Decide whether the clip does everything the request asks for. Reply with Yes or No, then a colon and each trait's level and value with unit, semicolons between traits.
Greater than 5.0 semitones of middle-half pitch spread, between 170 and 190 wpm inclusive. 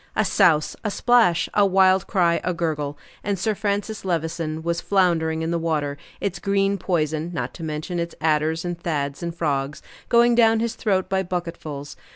No: average, 3.5 semitones; average, 180 wpm